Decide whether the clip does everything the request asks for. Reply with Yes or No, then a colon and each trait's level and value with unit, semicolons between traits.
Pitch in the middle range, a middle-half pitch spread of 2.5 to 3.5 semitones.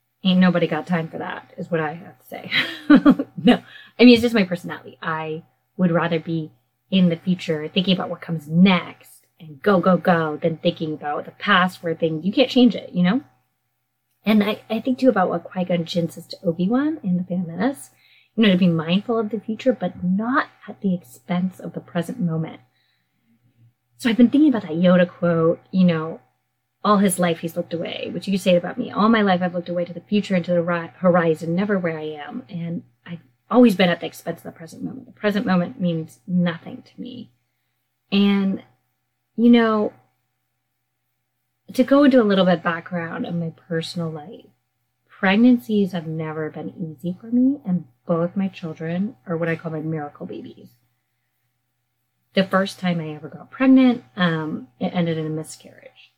No: medium, 175 Hz; average, 4.1 semitones